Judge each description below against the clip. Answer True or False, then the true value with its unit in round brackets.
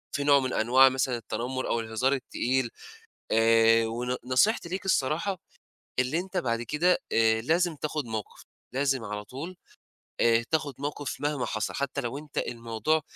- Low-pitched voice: True (130 Hz)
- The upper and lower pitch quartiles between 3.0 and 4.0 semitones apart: False (4.5 semitones)